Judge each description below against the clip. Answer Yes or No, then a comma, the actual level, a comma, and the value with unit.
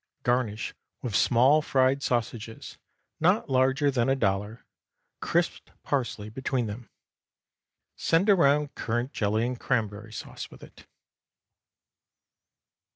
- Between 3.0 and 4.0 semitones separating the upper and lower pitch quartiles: Yes, average, 3.7 semitones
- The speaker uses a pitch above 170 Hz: No, low, 125 Hz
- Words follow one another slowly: Yes, slow, 105 wpm